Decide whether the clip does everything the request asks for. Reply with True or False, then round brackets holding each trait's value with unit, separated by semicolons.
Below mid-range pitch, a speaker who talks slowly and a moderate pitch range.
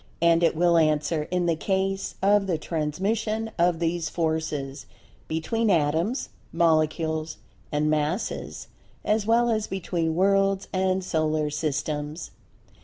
False (170 Hz; 120 wpm; 3.8 semitones)